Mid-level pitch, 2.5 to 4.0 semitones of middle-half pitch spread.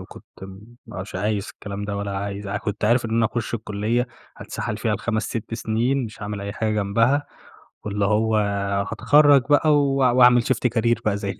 No: low, 110 Hz; average, 3.0 semitones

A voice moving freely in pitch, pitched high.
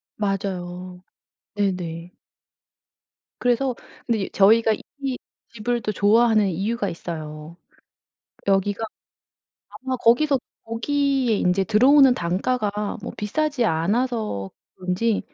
No: average, 4.9 semitones; high, 210 Hz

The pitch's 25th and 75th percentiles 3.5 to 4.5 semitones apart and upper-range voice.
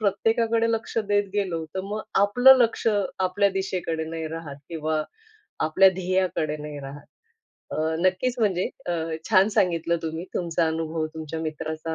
No: average, 4.1 semitones; medium, 175 Hz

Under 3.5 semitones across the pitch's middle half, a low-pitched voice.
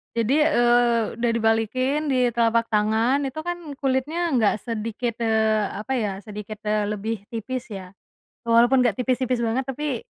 No: average, 2.9 semitones; high, 235 Hz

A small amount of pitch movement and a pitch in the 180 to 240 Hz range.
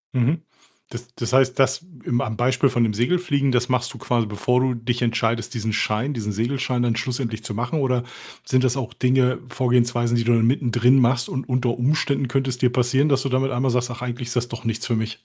No: narrow, 1.8 semitones; low, 125 Hz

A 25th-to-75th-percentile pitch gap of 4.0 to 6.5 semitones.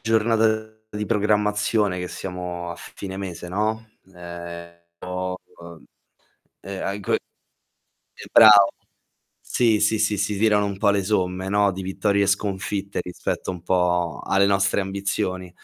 No: narrow, 2.4 semitones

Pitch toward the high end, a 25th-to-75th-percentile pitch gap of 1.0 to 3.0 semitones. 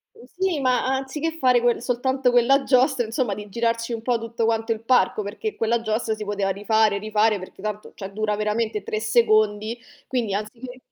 Yes: high, 230 Hz; average, 2.7 semitones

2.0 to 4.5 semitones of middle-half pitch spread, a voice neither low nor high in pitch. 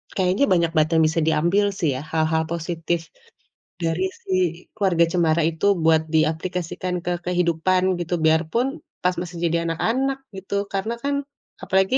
Yes: average, 2.7 semitones; medium, 170 Hz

